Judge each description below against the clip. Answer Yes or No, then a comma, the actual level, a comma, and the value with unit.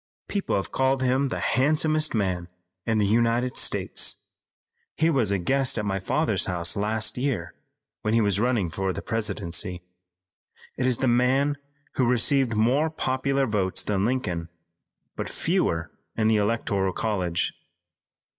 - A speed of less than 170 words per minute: Yes, average, 145 wpm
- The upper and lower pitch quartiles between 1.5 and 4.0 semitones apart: No, average, 5.1 semitones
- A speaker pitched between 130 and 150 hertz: No, low, 115 Hz